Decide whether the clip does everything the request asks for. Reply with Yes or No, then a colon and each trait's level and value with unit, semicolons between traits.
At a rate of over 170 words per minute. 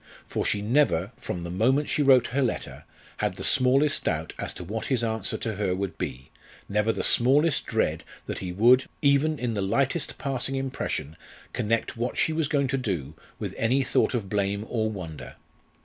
Yes: average, 190 wpm